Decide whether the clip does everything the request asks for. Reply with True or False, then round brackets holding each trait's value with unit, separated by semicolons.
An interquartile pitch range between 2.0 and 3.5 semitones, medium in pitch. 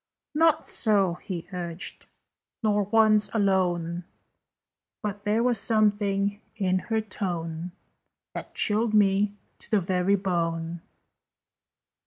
False (3.2 semitones; 200 Hz)